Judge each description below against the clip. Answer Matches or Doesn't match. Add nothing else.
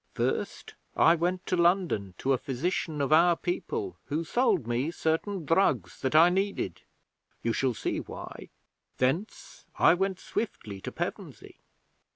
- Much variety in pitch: Matches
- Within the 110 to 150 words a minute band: Matches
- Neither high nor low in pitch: Matches